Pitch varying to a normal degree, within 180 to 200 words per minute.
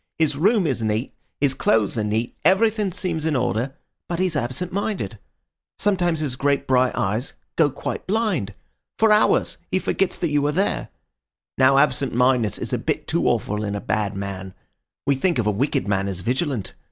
No: wide, 8.0 semitones; average, 190 wpm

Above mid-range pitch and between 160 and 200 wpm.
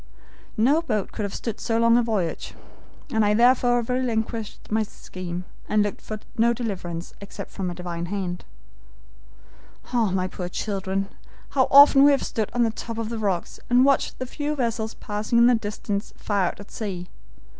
Yes: high, 220 Hz; average, 175 wpm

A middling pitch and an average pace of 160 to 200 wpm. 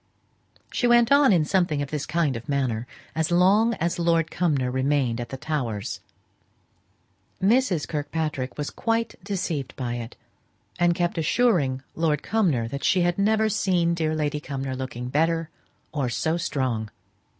No: medium, 155 Hz; average, 150 wpm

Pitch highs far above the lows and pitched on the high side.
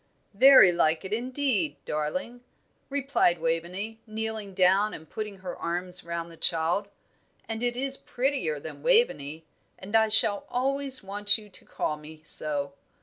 Yes: wide, 6.3 semitones; high, 200 Hz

